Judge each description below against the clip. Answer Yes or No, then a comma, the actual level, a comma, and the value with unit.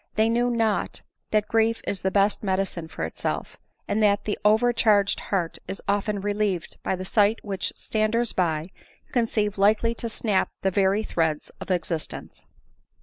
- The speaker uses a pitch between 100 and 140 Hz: No, high, 205 Hz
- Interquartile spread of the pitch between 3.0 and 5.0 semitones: No, narrow, 2.5 semitones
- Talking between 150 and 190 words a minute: Yes, average, 160 wpm